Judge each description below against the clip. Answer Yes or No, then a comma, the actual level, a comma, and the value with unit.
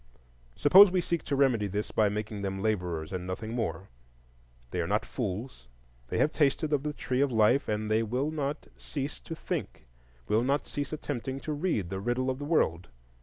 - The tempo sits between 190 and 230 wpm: Yes, average, 195 wpm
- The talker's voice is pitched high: No, low, 120 Hz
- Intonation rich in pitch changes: Yes, wide, 6.2 semitones